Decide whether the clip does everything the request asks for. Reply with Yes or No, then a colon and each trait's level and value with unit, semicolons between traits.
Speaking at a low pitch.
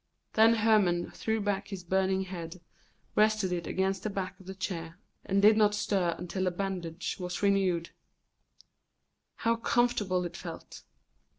No: high, 190 Hz